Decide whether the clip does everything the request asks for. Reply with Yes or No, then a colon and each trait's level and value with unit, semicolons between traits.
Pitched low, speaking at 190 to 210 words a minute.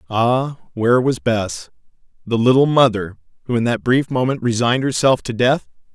No: low, 120 Hz; average, 160 wpm